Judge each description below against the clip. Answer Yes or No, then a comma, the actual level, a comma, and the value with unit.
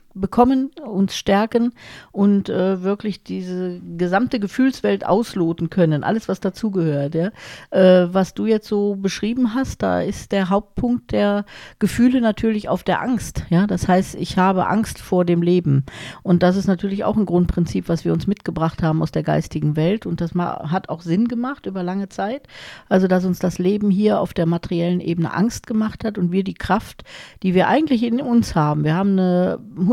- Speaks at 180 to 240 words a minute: Yes, average, 185 wpm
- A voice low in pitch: No, high, 190 Hz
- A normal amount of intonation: Yes, average, 3.4 semitones